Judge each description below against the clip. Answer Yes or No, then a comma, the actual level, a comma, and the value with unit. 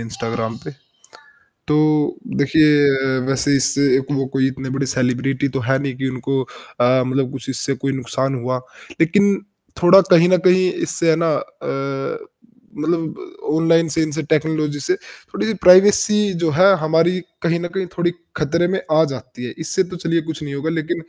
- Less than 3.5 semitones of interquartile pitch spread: No, average, 4.2 semitones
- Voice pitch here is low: No, medium, 150 Hz